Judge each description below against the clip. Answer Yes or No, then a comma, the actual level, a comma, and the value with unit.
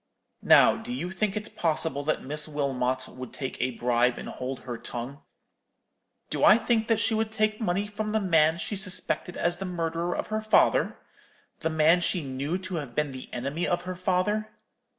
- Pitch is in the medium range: Yes, medium, 170 Hz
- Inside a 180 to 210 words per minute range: Yes, average, 190 wpm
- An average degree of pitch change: No, wide, 6.9 semitones